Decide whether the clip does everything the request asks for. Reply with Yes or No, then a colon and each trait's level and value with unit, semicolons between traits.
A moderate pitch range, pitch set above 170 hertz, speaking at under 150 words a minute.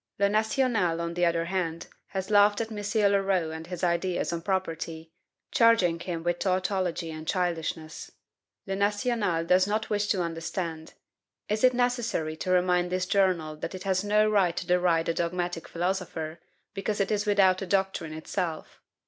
No: average, 3.3 semitones; medium, 185 Hz; average, 165 wpm